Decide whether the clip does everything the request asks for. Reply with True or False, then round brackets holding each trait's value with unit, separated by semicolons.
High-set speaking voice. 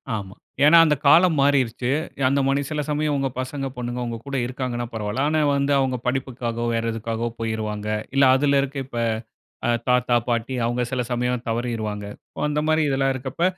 False (125 Hz)